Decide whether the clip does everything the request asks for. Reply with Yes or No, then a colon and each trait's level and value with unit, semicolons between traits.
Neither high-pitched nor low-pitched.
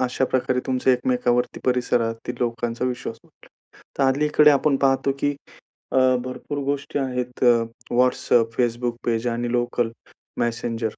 No: low, 125 Hz